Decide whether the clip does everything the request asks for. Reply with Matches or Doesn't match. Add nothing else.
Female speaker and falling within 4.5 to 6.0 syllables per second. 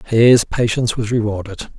Doesn't match